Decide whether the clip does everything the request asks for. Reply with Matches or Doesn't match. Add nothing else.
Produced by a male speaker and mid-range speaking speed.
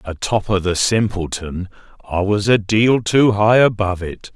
Matches